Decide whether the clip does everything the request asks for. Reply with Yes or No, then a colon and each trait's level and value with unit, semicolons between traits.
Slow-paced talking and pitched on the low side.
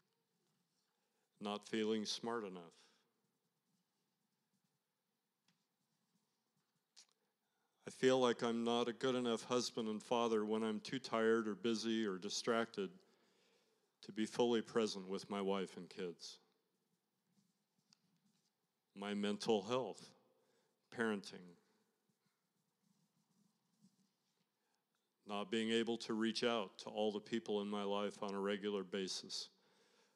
Yes: slow, 105 wpm; low, 130 Hz